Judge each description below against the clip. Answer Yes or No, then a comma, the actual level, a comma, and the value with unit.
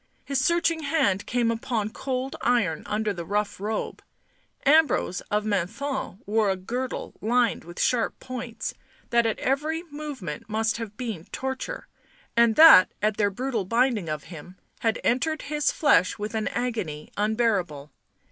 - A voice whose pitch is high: Yes, high, 225 Hz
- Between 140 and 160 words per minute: Yes, average, 145 wpm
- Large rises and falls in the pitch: No, average, 4.4 semitones